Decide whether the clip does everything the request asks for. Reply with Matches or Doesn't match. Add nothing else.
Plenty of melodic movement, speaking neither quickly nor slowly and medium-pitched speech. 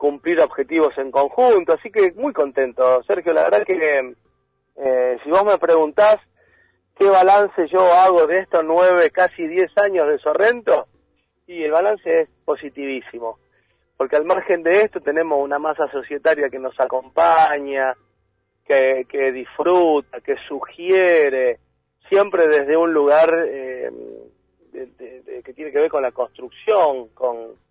Matches